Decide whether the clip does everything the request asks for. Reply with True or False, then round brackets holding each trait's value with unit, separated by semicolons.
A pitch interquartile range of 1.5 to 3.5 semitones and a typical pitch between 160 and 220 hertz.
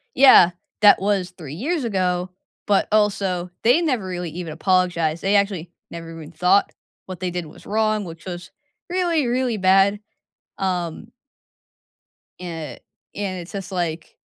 True (3.1 semitones; 185 Hz)